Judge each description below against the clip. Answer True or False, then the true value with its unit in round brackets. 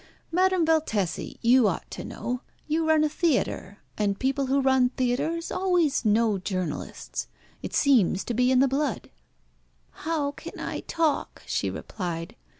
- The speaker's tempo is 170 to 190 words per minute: False (150 wpm)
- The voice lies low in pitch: False (265 Hz)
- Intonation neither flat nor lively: False (6.2 semitones)